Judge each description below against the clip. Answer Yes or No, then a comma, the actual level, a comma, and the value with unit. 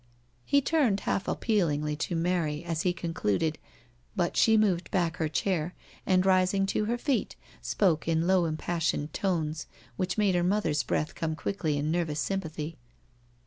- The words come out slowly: No, average, 160 wpm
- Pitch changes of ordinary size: Yes, average, 3.6 semitones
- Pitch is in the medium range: Yes, medium, 175 Hz